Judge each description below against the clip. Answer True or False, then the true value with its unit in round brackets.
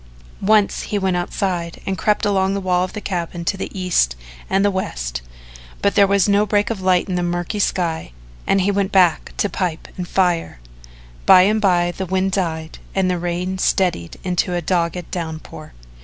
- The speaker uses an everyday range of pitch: False (2.1 semitones)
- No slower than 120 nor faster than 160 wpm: False (190 wpm)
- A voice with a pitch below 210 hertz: True (185 Hz)